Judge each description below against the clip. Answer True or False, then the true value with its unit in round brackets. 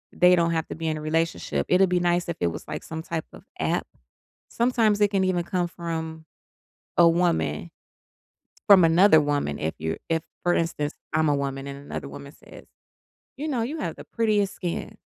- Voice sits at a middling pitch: True (170 Hz)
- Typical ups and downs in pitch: True (3.1 semitones)